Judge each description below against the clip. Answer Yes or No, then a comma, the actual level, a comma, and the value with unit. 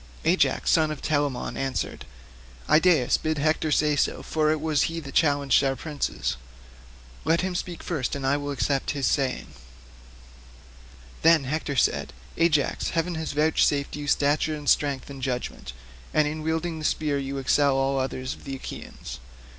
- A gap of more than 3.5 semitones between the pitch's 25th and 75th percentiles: No, narrow, 2.4 semitones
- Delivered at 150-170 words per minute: Yes, average, 160 wpm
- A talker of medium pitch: Yes, medium, 145 Hz